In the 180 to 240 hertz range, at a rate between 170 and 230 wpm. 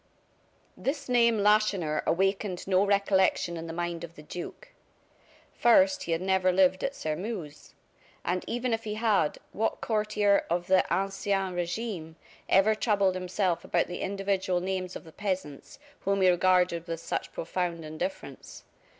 No: high, 190 Hz; average, 150 wpm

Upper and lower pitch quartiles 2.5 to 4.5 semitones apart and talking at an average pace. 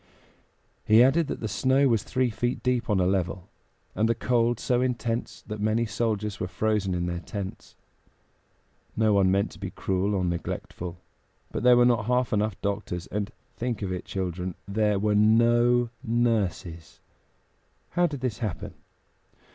Yes: average, 3.9 semitones; average, 165 wpm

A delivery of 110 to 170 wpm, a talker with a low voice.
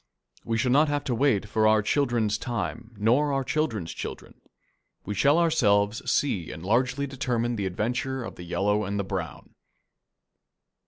Yes: average, 160 wpm; low, 115 Hz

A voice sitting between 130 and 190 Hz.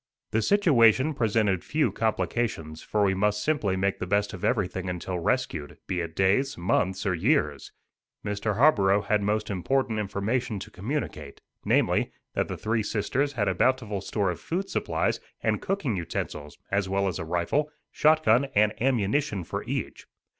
No: low, 105 Hz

